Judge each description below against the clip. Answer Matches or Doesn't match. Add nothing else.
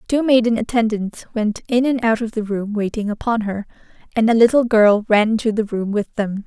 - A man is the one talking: Doesn't match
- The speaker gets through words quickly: Matches